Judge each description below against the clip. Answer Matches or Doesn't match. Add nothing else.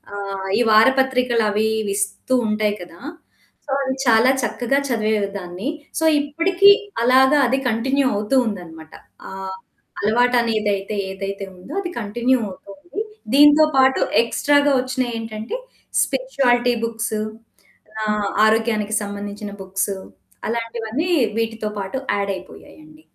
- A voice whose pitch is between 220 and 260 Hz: Matches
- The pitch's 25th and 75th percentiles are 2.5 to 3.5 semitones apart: Doesn't match